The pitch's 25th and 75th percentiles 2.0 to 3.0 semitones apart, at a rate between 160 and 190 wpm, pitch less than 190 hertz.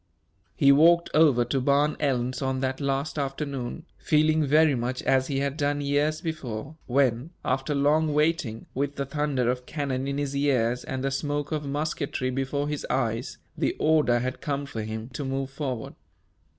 Yes: narrow, 2.4 semitones; average, 175 wpm; medium, 140 Hz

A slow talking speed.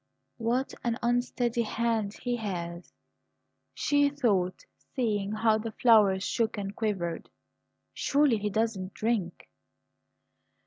Yes: slow, 105 wpm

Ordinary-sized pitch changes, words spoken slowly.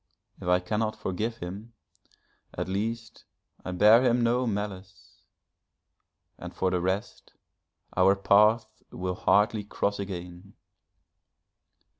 Yes: average, 3.0 semitones; slow, 110 wpm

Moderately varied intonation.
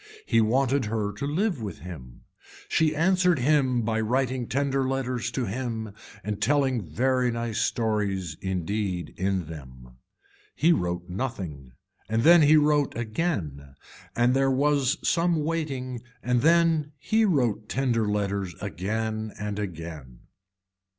No: wide, 6.0 semitones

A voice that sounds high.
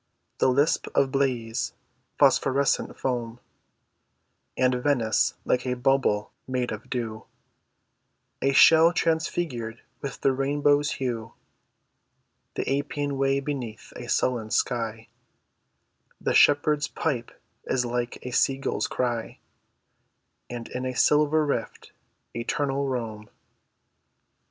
No: low, 130 Hz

